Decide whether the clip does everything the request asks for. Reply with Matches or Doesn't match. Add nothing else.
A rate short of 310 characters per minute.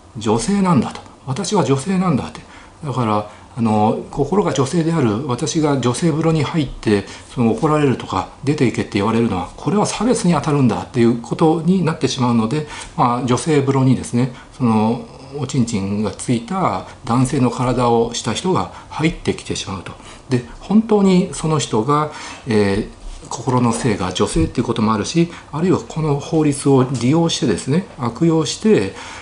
Doesn't match